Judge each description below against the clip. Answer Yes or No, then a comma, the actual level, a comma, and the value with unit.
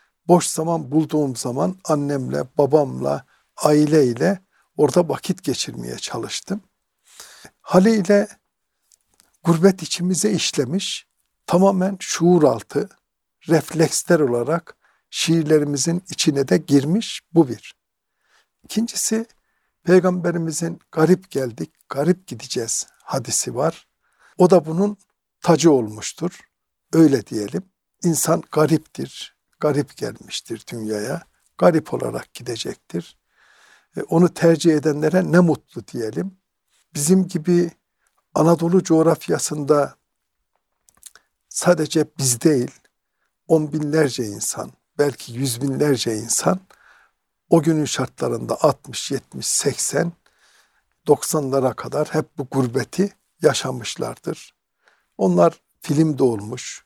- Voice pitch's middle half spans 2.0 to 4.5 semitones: Yes, average, 4.0 semitones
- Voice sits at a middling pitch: Yes, medium, 160 Hz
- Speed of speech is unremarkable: No, slow, 90 wpm